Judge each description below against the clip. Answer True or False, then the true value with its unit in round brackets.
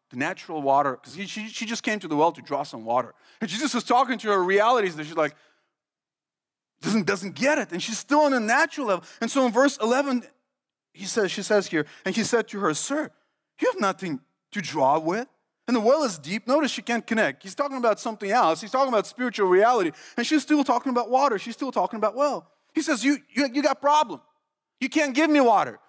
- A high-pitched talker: True (235 Hz)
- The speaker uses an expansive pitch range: True (6.0 semitones)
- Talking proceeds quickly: True (235 wpm)